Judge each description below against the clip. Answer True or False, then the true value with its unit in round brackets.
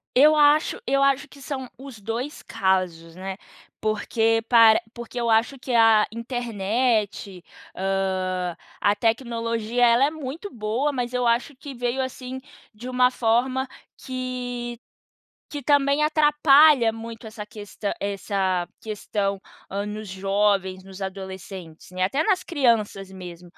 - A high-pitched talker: True (230 Hz)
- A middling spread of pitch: True (4.7 semitones)